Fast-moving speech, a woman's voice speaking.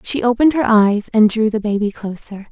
Yes: fast, 215 wpm; female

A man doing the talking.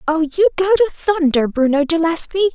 No: female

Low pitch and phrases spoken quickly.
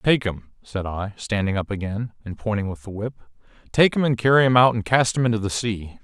Yes: low, 110 Hz; fast, 240 wpm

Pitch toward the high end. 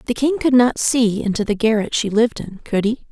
Yes: high, 230 Hz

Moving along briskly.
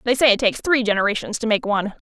Yes: fast, 260 wpm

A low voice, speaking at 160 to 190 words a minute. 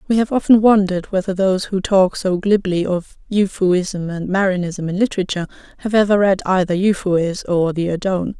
No: high, 190 Hz; average, 170 wpm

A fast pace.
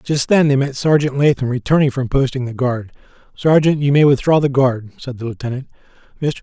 No: average, 195 wpm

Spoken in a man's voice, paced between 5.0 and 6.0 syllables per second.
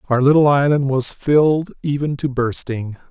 No: male; 4.6 syllables/s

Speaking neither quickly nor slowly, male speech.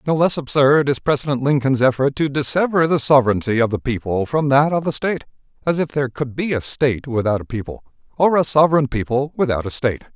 No: fast, 215 wpm; male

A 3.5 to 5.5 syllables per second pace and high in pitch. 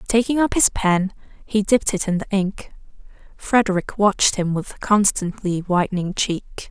Yes: 4.6 syllables/s; high, 200 Hz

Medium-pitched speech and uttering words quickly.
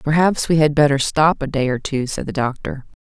Yes: medium, 145 Hz; fast, 235 wpm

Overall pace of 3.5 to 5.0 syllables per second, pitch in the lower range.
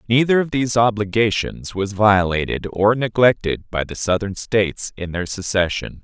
Yes: 4.8 syllables/s; low, 105 Hz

